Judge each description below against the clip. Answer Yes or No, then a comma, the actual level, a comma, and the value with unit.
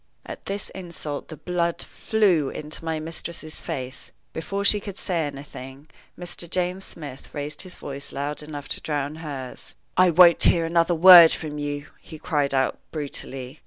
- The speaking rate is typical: Yes, average, 165 wpm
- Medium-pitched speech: Yes, medium, 155 Hz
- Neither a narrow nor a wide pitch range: Yes, average, 3.3 semitones